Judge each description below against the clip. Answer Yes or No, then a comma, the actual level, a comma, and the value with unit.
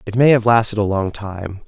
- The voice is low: Yes, low, 105 Hz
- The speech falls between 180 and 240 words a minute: No, fast, 250 wpm